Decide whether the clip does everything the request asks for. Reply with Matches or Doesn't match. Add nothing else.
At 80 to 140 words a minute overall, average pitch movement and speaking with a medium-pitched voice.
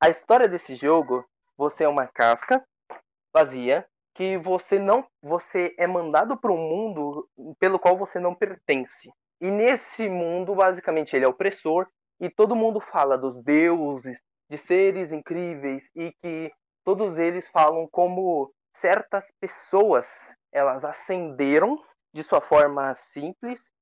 Matches